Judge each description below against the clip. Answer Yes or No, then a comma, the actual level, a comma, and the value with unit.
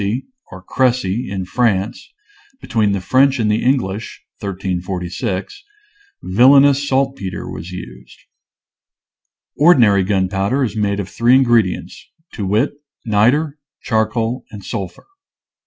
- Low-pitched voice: Yes, low, 105 Hz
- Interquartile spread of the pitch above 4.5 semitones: Yes, average, 5.1 semitones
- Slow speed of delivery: Yes, slow, 125 wpm